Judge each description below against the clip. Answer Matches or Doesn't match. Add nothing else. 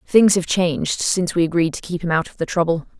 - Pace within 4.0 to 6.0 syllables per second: Doesn't match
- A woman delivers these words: Matches